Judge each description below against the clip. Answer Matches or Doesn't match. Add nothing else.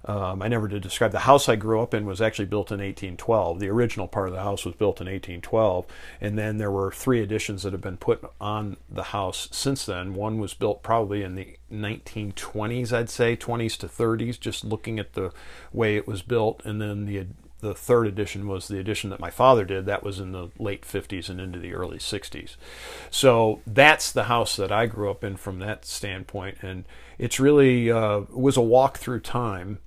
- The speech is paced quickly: Matches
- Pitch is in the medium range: Doesn't match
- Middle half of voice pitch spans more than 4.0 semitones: Doesn't match